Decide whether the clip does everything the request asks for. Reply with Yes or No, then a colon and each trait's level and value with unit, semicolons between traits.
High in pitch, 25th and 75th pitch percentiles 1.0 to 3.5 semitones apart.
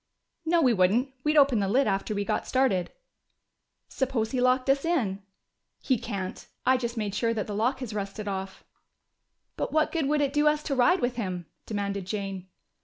No: high, 235 Hz; average, 5.2 semitones